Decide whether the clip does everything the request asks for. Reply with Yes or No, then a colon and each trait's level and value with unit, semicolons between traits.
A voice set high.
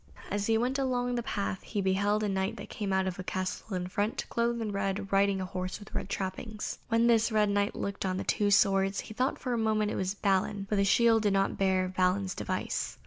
Yes: high, 200 Hz